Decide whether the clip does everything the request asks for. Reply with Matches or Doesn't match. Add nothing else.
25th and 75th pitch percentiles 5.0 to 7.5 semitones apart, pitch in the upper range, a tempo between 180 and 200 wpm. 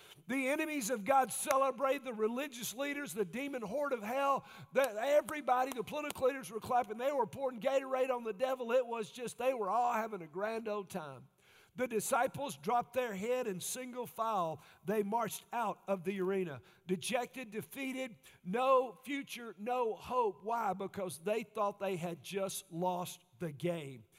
Doesn't match